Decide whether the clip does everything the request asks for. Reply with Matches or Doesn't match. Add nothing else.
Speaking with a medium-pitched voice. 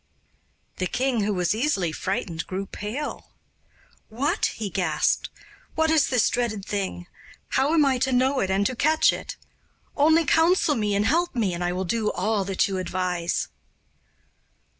Doesn't match